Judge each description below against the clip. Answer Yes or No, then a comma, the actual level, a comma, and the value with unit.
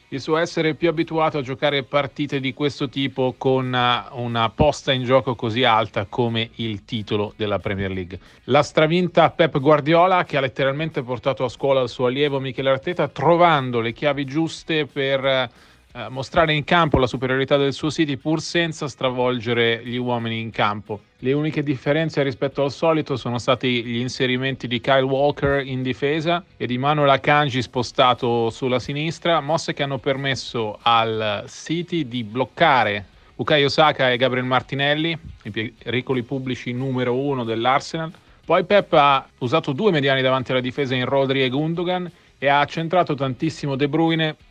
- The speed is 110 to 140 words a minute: No, average, 160 wpm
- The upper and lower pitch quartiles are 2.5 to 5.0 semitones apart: Yes, average, 3.5 semitones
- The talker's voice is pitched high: No, low, 135 Hz